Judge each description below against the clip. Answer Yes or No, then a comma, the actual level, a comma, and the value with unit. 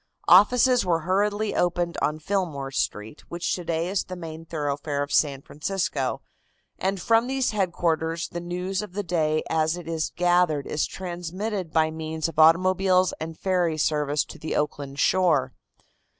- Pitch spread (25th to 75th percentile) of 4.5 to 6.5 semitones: No, average, 3.1 semitones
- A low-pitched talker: No, medium, 170 Hz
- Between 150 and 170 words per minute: Yes, average, 155 wpm